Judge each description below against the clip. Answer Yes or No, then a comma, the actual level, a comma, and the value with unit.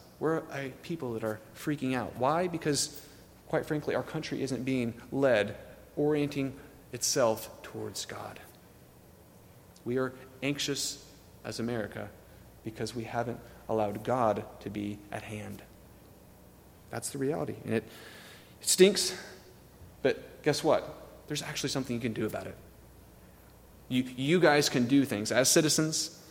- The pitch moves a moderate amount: Yes, average, 4.8 semitones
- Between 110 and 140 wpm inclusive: Yes, slow, 135 wpm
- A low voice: Yes, low, 125 Hz